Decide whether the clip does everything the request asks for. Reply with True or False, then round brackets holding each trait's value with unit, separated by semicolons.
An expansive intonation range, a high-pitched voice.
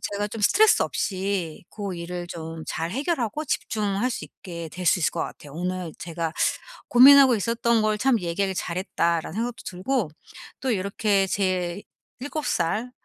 False (5.0 semitones; 195 Hz)